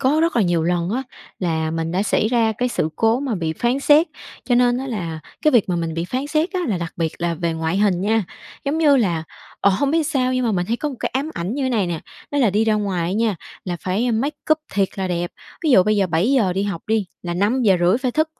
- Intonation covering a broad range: Yes, wide, 6.5 semitones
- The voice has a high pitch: Yes, high, 210 Hz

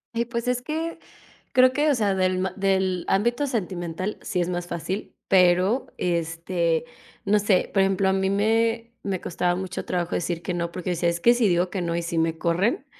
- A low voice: No, high, 190 Hz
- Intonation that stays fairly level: No, average, 4.3 semitones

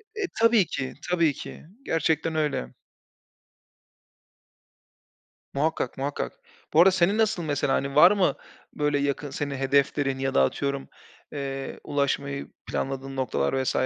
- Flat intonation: No, average, 3.0 semitones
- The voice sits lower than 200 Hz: Yes, medium, 140 Hz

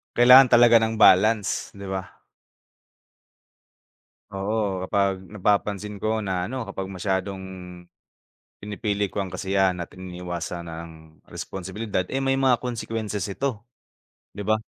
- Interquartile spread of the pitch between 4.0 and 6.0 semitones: No, average, 2.9 semitones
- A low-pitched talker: Yes, low, 100 Hz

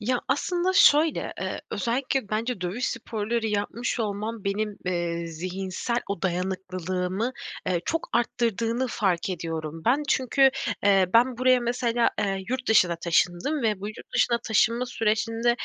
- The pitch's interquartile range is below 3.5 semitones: No, average, 4.5 semitones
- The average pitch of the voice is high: Yes, high, 220 Hz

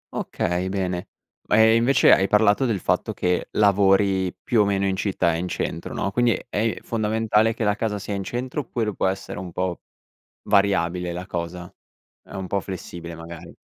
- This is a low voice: Yes, low, 100 Hz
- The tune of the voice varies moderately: Yes, average, 3.0 semitones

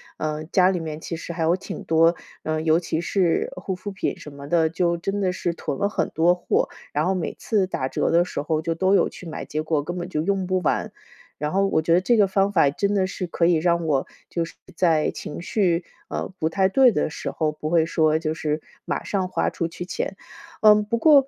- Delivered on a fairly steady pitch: No, average, 3.2 semitones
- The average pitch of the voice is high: No, medium, 170 Hz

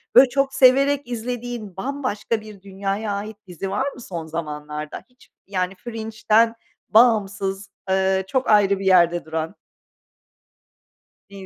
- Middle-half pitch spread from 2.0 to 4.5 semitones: Yes, average, 4.1 semitones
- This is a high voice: Yes, high, 205 Hz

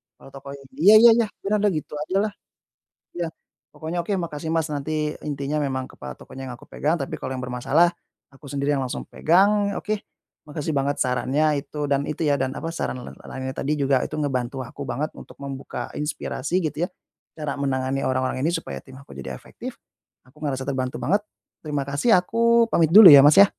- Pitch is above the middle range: No, medium, 145 Hz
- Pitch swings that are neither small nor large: Yes, average, 3.8 semitones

